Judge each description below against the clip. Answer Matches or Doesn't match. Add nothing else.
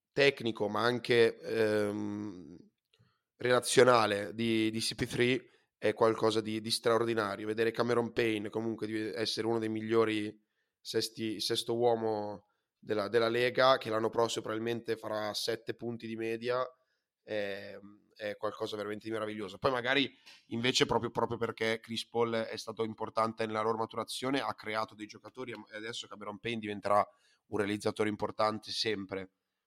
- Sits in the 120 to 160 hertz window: Doesn't match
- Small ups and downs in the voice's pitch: Matches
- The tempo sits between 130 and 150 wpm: Matches